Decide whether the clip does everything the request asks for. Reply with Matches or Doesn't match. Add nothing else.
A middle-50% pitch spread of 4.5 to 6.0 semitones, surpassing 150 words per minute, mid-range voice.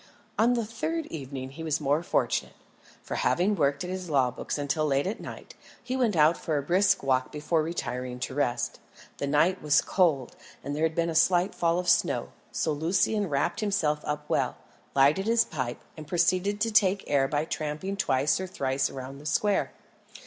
Matches